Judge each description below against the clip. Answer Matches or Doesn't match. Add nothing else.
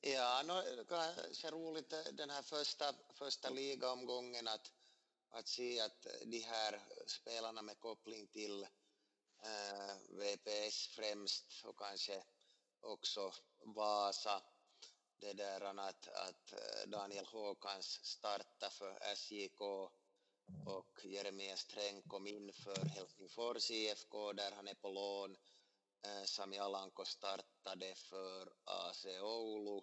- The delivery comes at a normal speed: Doesn't match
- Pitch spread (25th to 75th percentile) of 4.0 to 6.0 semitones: Doesn't match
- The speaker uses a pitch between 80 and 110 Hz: Matches